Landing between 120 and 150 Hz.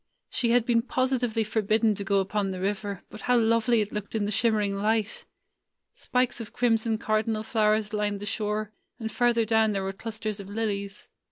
No: high, 215 Hz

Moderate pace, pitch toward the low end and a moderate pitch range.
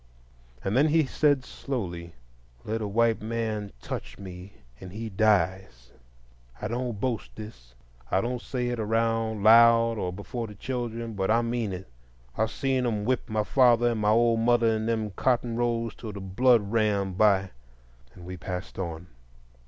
Yes: average, 160 wpm; low, 110 Hz; average, 3.4 semitones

